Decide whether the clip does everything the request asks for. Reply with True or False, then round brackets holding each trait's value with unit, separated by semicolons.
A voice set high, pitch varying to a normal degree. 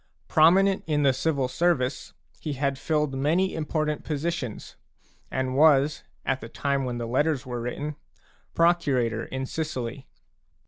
False (140 Hz; 3.4 semitones)